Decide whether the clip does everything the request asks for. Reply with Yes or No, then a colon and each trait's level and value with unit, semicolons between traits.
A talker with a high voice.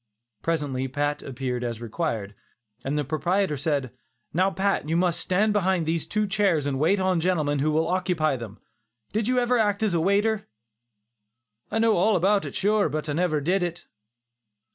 No: medium, 170 Hz